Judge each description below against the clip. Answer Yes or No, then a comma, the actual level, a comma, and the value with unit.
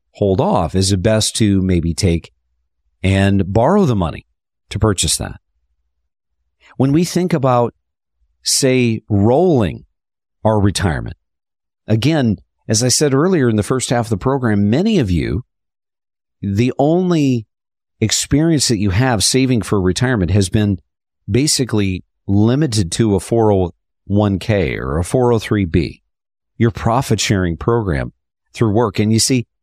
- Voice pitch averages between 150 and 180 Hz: No, low, 105 Hz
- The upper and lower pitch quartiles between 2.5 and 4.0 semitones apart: No, average, 5.2 semitones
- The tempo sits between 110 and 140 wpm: Yes, slow, 135 wpm